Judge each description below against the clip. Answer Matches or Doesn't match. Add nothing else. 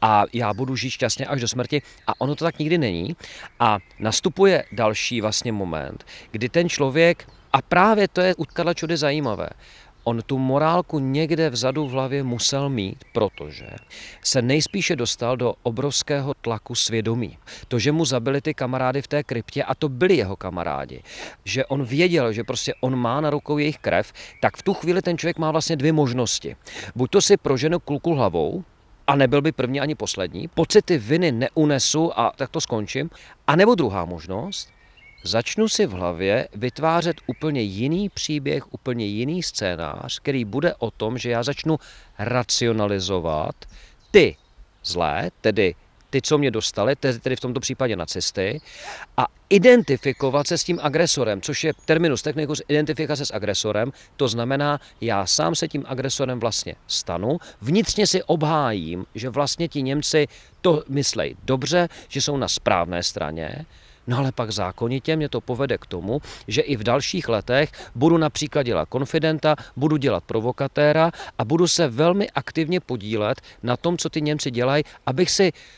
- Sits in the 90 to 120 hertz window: Doesn't match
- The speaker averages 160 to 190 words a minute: Matches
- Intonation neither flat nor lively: Matches